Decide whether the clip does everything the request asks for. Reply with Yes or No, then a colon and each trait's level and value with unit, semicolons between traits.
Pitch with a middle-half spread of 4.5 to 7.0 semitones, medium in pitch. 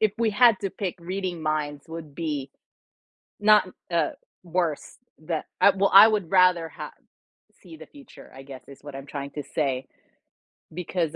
Yes: average, 4.9 semitones; medium, 170 Hz